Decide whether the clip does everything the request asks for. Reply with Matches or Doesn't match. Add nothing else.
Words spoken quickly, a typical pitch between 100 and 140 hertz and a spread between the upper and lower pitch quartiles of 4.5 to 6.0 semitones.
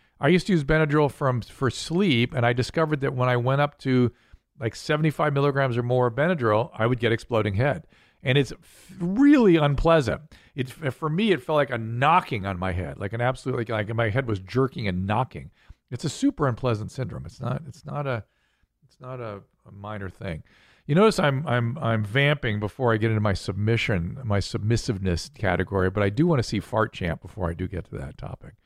Matches